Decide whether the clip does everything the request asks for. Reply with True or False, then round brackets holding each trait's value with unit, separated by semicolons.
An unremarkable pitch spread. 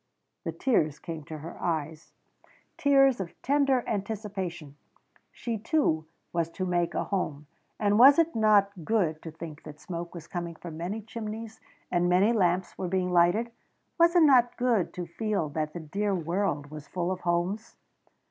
True (4.8 semitones)